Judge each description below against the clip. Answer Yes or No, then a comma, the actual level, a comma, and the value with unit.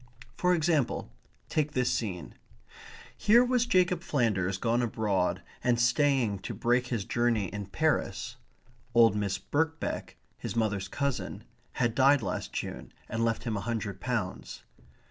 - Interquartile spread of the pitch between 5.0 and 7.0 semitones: Yes, wide, 5.6 semitones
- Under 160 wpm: Yes, average, 140 wpm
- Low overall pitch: Yes, low, 120 Hz